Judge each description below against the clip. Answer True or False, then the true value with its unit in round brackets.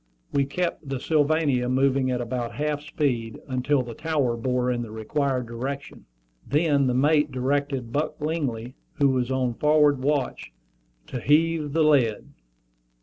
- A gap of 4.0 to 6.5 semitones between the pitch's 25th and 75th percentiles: False (3.0 semitones)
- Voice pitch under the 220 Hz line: True (135 Hz)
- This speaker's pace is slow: False (145 wpm)